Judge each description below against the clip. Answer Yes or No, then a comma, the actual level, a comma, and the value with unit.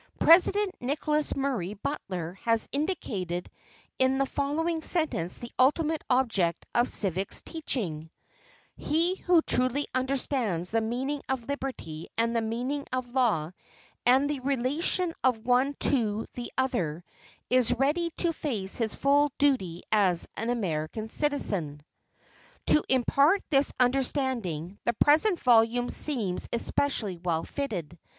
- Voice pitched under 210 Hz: No, very high, 250 Hz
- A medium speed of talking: No, slow, 125 wpm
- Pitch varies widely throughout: Yes, wide, 5.7 semitones